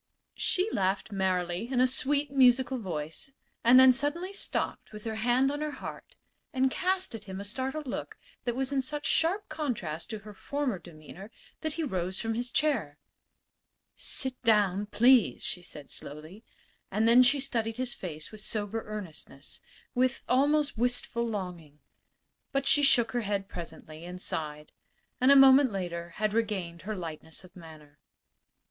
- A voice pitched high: Yes, high, 225 Hz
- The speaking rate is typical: Yes, average, 165 wpm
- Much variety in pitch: Yes, wide, 6.5 semitones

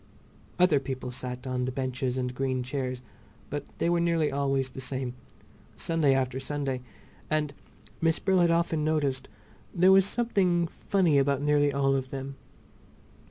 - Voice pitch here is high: No, medium, 140 Hz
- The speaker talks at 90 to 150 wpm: Yes, average, 145 wpm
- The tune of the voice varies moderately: Yes, average, 4.0 semitones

